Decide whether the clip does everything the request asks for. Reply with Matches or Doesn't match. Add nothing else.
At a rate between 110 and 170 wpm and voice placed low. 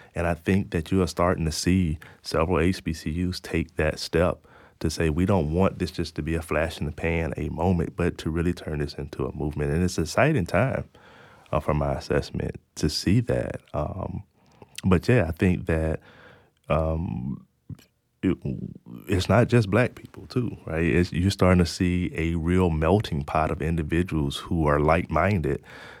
Doesn't match